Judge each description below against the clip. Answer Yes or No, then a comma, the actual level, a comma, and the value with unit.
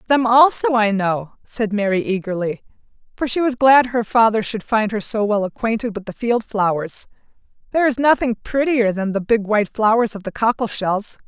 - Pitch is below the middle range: No, high, 220 Hz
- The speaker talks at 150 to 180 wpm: No, average, 190 wpm